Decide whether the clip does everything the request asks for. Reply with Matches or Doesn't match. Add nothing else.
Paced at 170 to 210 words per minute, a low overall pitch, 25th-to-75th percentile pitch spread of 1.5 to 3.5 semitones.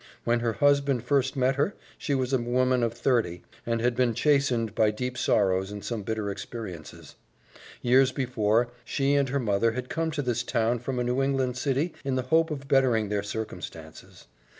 Matches